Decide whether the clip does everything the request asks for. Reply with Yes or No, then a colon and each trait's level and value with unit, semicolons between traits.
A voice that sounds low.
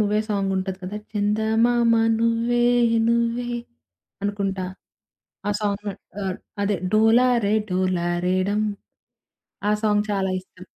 No: high, 205 Hz